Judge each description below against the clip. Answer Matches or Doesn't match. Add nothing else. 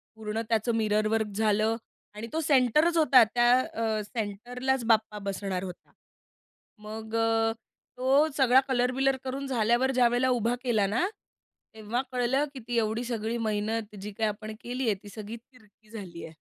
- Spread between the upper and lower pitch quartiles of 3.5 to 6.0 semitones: Doesn't match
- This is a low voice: Doesn't match